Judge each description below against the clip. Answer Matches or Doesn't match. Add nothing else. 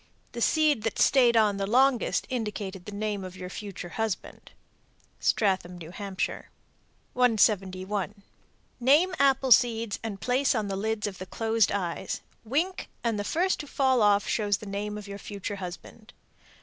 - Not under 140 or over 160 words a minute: Matches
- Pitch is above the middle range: Matches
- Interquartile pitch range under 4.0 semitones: Matches